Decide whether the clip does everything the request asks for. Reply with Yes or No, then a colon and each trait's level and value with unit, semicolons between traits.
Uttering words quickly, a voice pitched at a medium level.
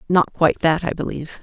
Yes: fast, 210 wpm; medium, 165 Hz